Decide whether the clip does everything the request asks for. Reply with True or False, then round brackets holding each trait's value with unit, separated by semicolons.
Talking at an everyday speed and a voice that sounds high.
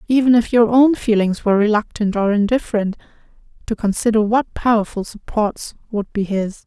True (155 wpm; 215 Hz)